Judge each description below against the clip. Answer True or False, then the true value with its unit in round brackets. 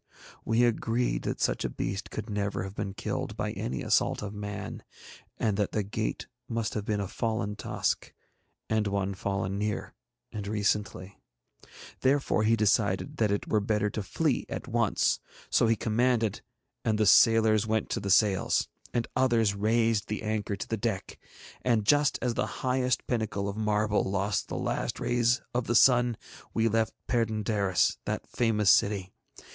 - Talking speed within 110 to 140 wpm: False (165 wpm)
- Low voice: True (110 Hz)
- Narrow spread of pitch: True (2.2 semitones)